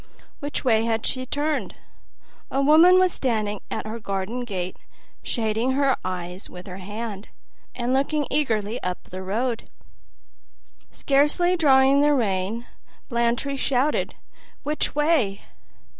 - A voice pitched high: Yes, high, 240 Hz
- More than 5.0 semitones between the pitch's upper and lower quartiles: Yes, wide, 5.4 semitones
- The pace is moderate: No, slow, 125 wpm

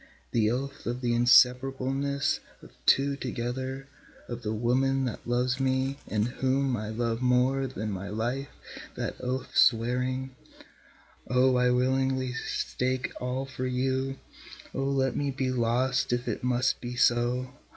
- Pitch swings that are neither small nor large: No, narrow, 1.6 semitones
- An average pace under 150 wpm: Yes, average, 140 wpm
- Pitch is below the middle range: Yes, low, 130 Hz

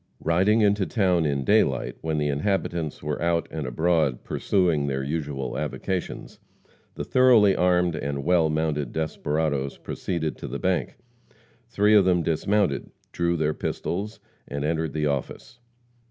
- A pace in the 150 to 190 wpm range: No, average, 140 wpm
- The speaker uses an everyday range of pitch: Yes, average, 4.0 semitones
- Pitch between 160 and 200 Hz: No, very low, 80 Hz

